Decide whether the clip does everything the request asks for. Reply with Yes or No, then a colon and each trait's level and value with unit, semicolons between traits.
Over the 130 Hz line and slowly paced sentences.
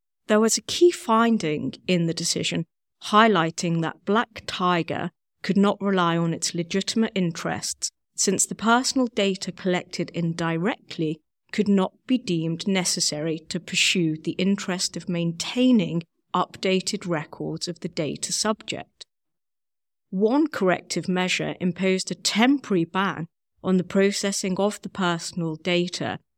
Yes: medium, 185 Hz; slow, 125 wpm